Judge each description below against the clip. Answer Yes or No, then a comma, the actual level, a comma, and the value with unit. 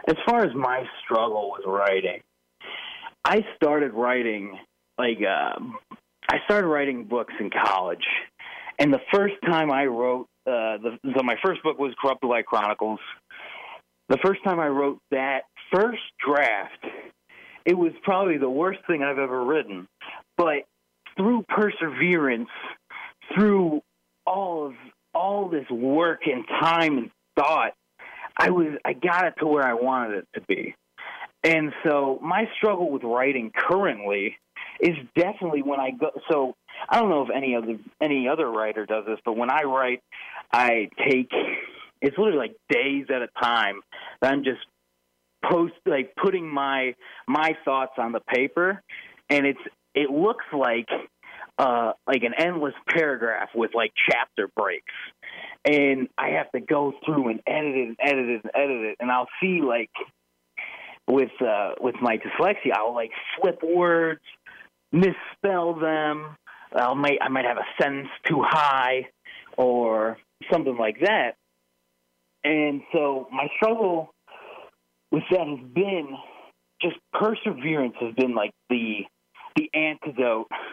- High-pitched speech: No, low, 135 Hz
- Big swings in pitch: Yes, wide, 5.7 semitones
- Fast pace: No, average, 145 wpm